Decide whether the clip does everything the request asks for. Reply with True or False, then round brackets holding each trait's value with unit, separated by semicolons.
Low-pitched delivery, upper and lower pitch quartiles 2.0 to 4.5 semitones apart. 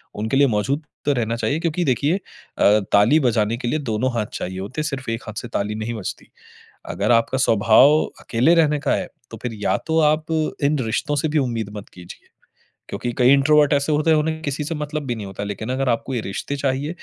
False (130 Hz; 5.1 semitones)